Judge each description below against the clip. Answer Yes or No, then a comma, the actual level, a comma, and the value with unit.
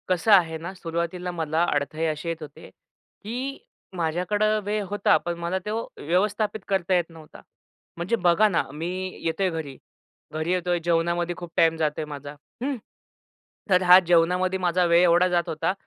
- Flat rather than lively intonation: Yes, narrow, 2.2 semitones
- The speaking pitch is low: No, medium, 175 Hz